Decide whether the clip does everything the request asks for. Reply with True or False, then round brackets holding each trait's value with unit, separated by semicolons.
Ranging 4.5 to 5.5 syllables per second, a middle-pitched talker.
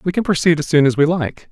False (6.4 syllables/s; 160 Hz)